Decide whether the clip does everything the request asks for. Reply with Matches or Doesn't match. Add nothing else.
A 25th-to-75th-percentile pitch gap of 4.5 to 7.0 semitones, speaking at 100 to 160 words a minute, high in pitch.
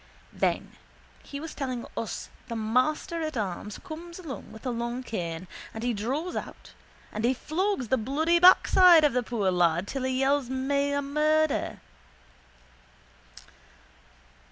Matches